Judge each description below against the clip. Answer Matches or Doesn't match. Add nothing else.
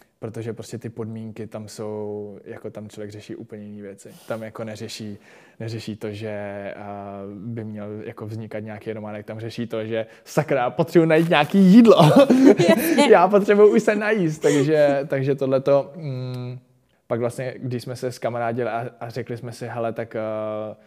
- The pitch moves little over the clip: Doesn't match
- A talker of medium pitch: Doesn't match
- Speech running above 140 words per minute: Matches